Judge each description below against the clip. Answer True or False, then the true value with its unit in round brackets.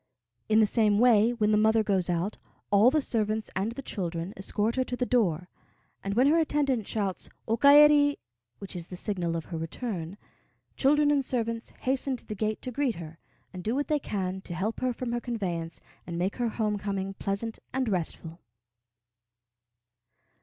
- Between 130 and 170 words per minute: False (185 wpm)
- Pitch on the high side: True (215 Hz)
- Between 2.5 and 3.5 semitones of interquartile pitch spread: False (4.7 semitones)